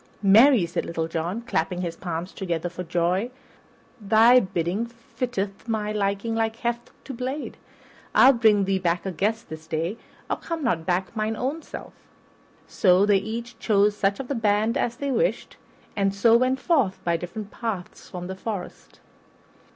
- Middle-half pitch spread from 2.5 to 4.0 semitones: No, average, 4.5 semitones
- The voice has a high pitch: Yes, high, 205 Hz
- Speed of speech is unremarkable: Yes, average, 165 wpm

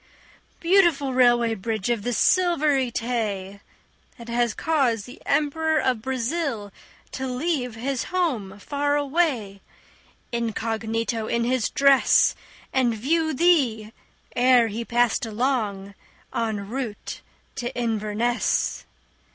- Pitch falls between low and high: No, high, 240 Hz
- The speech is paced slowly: Yes, slow, 110 wpm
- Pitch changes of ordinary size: Yes, average, 3.9 semitones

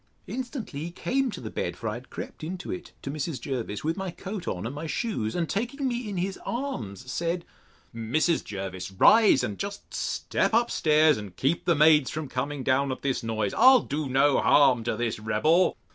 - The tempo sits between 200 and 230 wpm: Yes, fast, 205 wpm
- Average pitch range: No, wide, 7.7 semitones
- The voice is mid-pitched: Yes, medium, 150 Hz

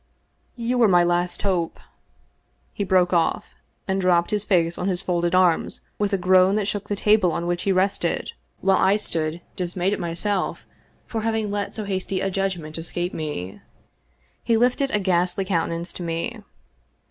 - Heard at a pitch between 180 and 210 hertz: Yes, medium, 185 Hz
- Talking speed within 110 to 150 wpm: No, average, 175 wpm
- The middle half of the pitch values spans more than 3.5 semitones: No, average, 2.7 semitones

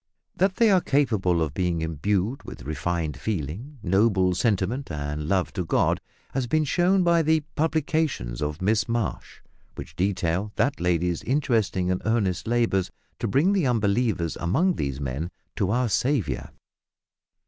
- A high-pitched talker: No, low, 100 Hz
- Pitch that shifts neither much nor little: No, wide, 7.8 semitones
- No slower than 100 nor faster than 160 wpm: Yes, average, 150 wpm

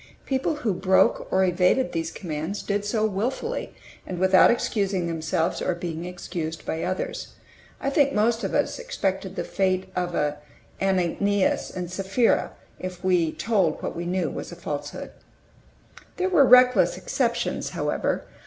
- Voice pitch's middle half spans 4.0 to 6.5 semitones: Yes, average, 4.4 semitones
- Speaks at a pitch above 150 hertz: Yes, high, 190 Hz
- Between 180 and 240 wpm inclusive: No, average, 145 wpm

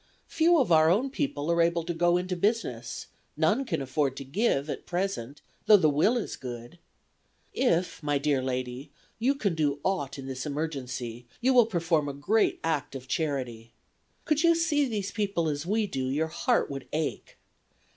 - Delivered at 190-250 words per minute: No, average, 180 wpm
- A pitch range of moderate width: No, wide, 7.0 semitones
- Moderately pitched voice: Yes, medium, 160 Hz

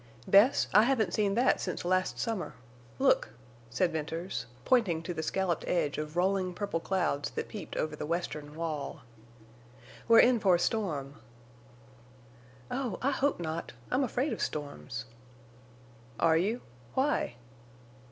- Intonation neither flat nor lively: No, wide, 5.7 semitones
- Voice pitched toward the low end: No, medium, 180 Hz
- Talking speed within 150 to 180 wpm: No, average, 140 wpm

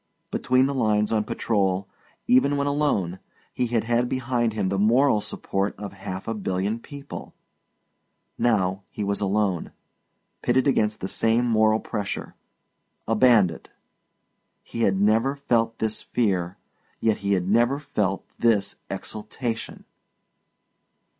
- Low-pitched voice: Yes, low, 110 Hz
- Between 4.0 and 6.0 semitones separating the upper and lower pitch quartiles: No, average, 3.4 semitones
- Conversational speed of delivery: No, slow, 130 wpm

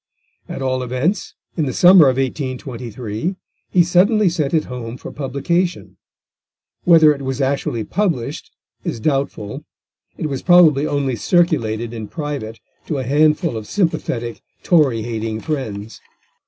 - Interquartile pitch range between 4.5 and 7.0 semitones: Yes, wide, 5.5 semitones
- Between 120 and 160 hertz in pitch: Yes, low, 135 Hz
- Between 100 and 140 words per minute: Yes, slow, 135 wpm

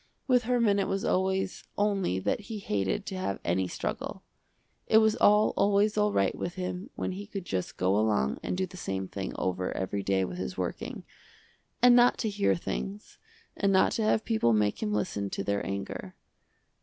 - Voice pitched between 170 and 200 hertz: Yes, medium, 185 Hz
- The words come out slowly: No, average, 195 wpm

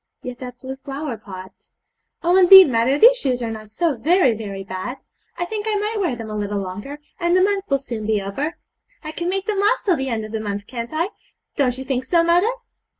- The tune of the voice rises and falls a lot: Yes, wide, 8.0 semitones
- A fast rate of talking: Yes, fast, 230 wpm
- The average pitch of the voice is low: No, very high, 265 Hz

